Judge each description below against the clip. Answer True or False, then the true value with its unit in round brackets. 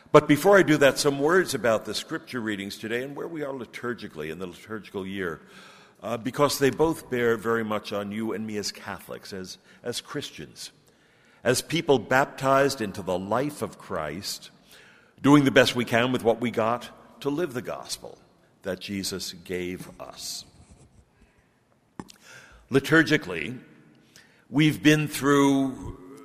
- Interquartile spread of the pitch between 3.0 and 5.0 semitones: False (5.4 semitones)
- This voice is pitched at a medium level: False (120 Hz)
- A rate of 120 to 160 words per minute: True (150 wpm)